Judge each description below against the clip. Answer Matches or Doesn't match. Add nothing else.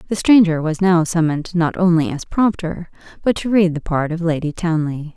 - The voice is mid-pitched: Matches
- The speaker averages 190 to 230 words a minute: Matches